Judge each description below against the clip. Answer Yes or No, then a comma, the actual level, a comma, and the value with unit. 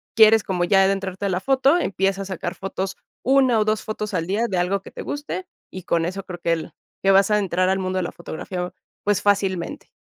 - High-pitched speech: Yes, high, 195 Hz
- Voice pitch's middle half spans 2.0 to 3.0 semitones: Yes, narrow, 2.5 semitones